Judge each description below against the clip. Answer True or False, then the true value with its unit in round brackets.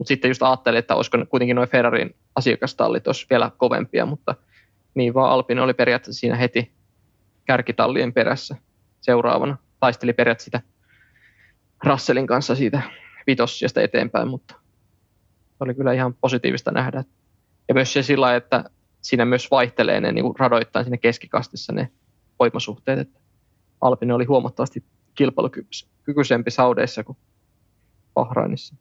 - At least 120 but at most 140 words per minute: True (125 wpm)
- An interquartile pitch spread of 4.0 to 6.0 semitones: False (3.0 semitones)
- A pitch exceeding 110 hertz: True (120 Hz)